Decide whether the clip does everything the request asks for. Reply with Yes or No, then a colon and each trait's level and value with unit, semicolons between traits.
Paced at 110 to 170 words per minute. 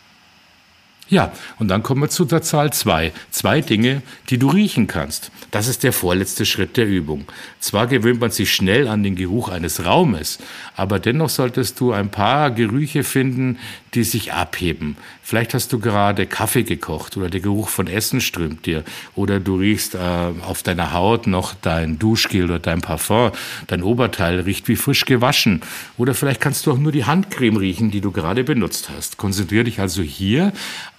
No: average, 180 wpm